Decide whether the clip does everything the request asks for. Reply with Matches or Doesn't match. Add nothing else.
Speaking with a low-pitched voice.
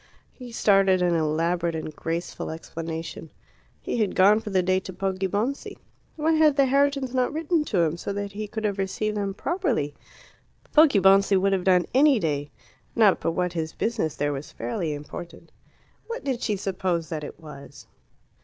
Doesn't match